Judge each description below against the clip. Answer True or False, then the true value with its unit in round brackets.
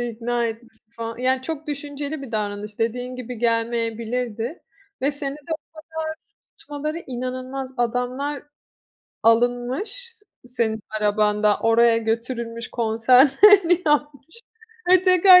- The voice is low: False (250 Hz)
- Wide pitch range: False (4.3 semitones)